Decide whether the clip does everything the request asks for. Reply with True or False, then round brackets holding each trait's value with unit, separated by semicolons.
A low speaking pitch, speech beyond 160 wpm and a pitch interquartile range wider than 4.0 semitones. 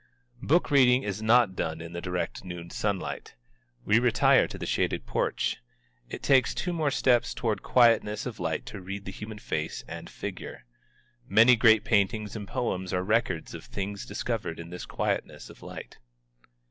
True (105 Hz; 170 wpm; 4.4 semitones)